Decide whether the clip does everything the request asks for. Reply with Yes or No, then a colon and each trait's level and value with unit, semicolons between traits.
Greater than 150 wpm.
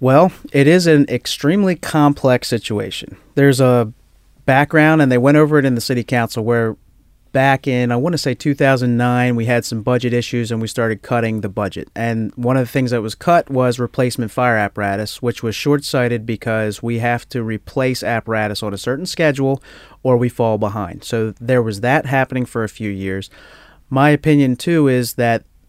Yes: average, 190 wpm